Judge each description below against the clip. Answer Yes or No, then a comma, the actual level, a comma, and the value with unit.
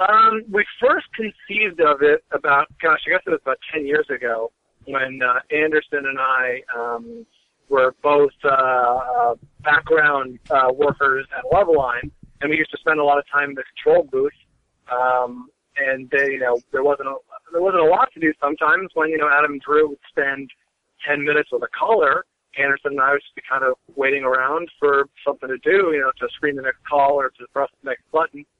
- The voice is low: No, medium, 145 Hz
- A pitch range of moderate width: No, wide, 5.9 semitones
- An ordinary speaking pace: No, fast, 210 wpm